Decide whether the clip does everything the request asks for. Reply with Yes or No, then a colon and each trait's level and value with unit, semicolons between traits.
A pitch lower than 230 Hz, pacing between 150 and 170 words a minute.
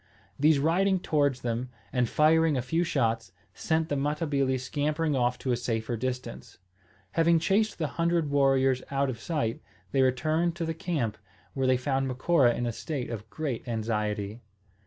Yes: low, 135 Hz; average, 165 wpm